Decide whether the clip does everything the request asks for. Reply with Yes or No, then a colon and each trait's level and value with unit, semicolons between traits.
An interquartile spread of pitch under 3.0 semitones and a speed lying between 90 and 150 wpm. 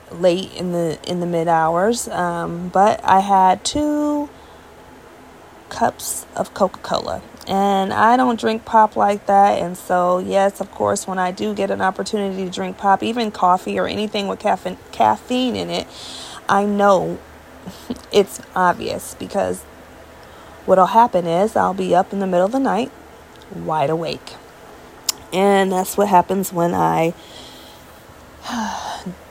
Yes: narrow, 2.4 semitones; average, 140 wpm